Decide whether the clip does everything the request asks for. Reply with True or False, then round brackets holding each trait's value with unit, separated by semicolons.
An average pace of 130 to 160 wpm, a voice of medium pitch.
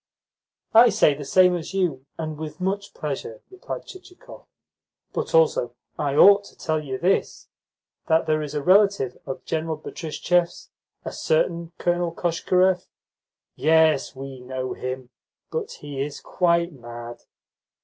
True (140 wpm; 160 Hz)